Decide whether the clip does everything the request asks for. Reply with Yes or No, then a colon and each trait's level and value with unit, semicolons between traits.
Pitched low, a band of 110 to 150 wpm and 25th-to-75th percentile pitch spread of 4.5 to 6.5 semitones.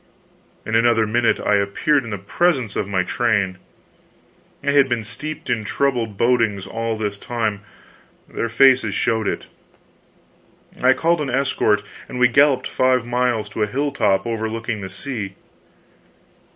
No: low, 115 Hz; average, 145 wpm; average, 3.5 semitones